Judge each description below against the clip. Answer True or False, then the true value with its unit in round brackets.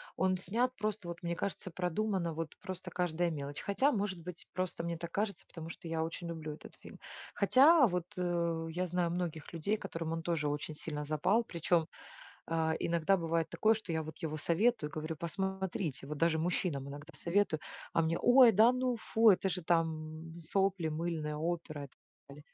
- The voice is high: False (170 Hz)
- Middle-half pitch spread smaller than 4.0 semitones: True (3.2 semitones)